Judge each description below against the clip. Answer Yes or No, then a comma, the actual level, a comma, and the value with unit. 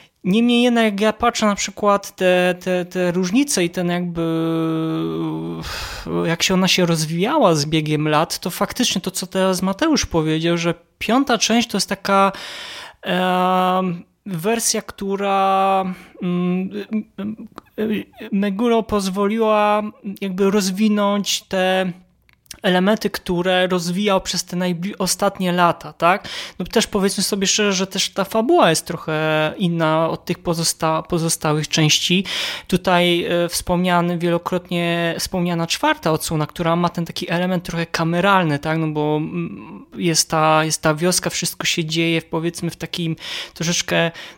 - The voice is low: No, medium, 180 Hz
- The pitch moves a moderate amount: Yes, average, 3.1 semitones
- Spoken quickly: No, average, 130 wpm